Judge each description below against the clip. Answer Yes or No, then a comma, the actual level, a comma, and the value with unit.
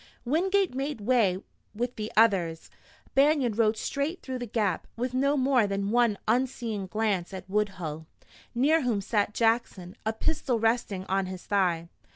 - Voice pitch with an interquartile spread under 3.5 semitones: No, average, 4.6 semitones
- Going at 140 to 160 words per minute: Yes, average, 155 wpm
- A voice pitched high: Yes, high, 225 Hz